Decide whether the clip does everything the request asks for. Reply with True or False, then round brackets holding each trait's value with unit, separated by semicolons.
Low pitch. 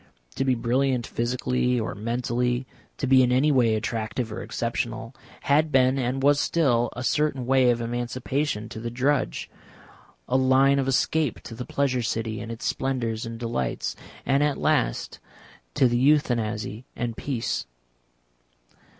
True (125 Hz)